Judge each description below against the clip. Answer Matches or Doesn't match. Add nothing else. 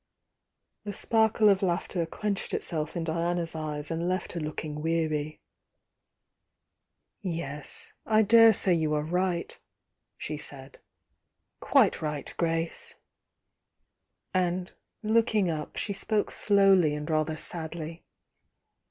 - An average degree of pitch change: Matches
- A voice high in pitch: Doesn't match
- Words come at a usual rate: Doesn't match